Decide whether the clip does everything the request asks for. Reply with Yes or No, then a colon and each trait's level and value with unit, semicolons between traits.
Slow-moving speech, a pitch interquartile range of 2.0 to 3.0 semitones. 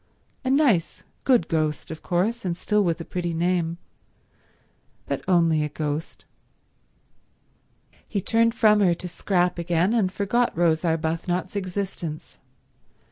No: slow, 130 wpm; average, 3.6 semitones